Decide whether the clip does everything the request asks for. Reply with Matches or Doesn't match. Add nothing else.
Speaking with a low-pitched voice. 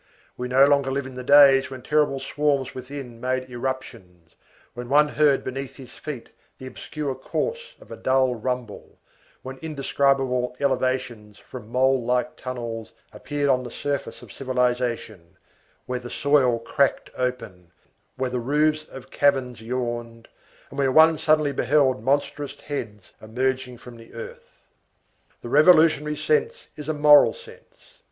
Matches